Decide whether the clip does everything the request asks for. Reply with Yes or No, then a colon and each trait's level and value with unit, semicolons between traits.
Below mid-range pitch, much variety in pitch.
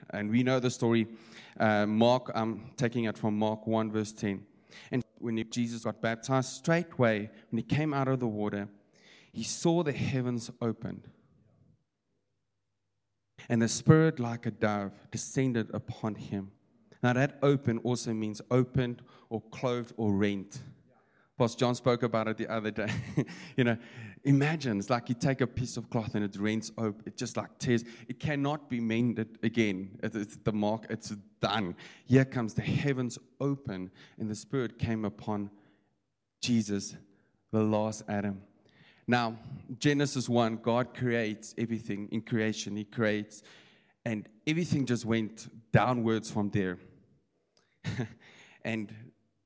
No: low, 115 Hz; average, 2.7 semitones